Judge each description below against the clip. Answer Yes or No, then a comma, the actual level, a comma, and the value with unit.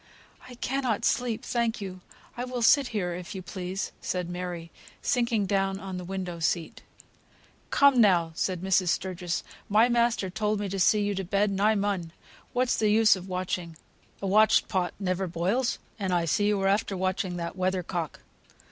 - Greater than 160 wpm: Yes, average, 185 wpm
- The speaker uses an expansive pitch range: No, average, 3.1 semitones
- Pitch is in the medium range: No, high, 195 Hz